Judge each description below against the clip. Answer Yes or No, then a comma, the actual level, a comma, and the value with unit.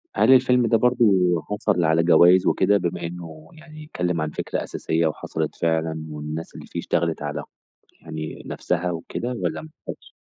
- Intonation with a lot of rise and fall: Yes, wide, 6.1 semitones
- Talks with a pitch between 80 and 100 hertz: Yes, very low, 85 Hz